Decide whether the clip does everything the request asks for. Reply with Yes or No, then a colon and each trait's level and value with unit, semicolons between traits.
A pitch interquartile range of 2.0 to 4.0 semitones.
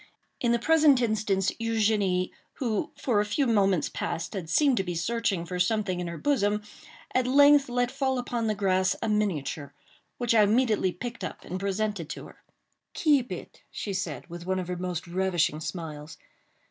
No: average, 4.8 semitones